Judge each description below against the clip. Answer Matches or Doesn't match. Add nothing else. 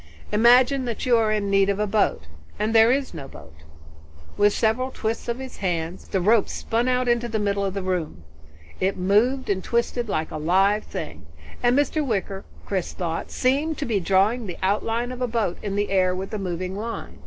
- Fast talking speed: Matches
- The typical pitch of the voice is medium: Doesn't match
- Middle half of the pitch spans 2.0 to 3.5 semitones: Doesn't match